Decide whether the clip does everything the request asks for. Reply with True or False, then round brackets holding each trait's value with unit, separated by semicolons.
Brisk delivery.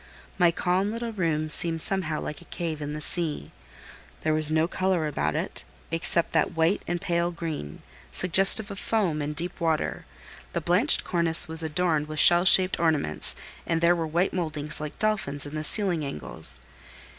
False (175 wpm)